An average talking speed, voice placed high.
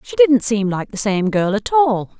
No: fast, 245 wpm; high, 230 Hz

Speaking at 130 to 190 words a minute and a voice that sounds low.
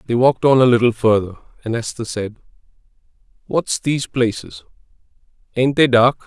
Yes: average, 145 wpm; low, 120 Hz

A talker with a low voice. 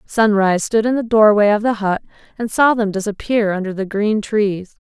No: high, 210 Hz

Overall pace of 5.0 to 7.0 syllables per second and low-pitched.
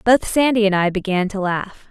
No: 5.1 syllables/s; high, 200 Hz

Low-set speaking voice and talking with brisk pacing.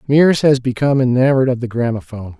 No: low, 125 Hz; average, 175 wpm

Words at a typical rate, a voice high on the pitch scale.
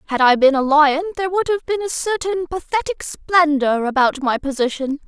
Yes: average, 190 wpm; very high, 315 Hz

